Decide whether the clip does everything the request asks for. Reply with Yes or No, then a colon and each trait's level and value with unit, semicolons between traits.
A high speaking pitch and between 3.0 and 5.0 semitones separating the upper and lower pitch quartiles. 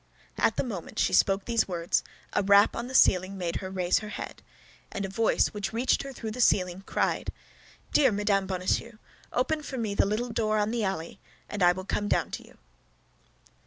Yes: high, 205 Hz; average, 3.4 semitones